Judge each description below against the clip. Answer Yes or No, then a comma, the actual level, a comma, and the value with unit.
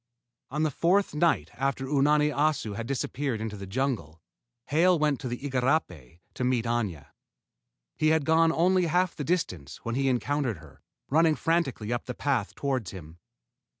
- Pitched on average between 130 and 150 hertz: Yes, low, 135 Hz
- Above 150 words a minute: Yes, average, 165 wpm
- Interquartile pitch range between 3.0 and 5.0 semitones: No, wide, 5.6 semitones